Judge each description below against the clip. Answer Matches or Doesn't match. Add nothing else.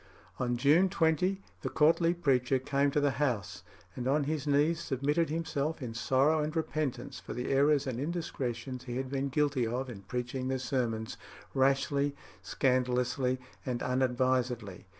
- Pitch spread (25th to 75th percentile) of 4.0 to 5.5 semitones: Doesn't match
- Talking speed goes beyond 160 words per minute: Doesn't match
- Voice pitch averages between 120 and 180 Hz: Matches